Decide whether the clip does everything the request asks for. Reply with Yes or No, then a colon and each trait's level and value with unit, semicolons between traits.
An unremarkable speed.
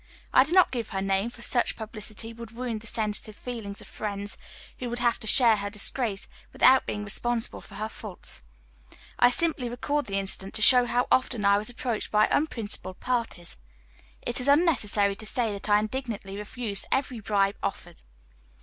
Yes: average, 180 wpm